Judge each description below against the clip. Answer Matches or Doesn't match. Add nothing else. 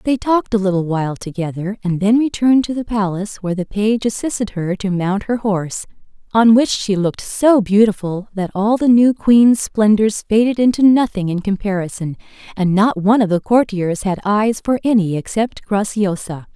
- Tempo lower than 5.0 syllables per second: Doesn't match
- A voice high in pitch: Matches